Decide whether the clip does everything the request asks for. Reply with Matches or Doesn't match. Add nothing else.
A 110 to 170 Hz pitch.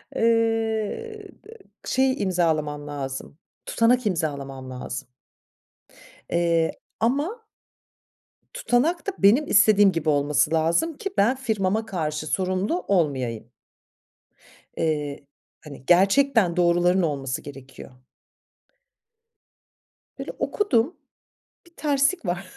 Doesn't match